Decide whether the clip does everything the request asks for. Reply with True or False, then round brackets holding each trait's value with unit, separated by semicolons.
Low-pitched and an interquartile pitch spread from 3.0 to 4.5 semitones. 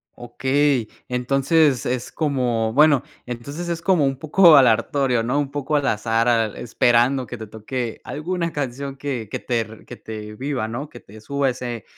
True (130 Hz; 3.6 semitones)